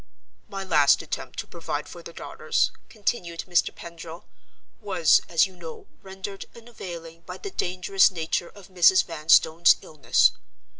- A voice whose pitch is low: No, medium, 175 Hz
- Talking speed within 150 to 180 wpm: No, average, 140 wpm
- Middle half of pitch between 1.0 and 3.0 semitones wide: Yes, narrow, 2.6 semitones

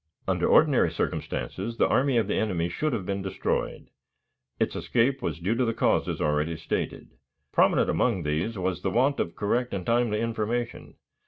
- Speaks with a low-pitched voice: Yes, low, 105 Hz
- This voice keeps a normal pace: Yes, average, 170 wpm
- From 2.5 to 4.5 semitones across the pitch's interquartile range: No, average, 5.1 semitones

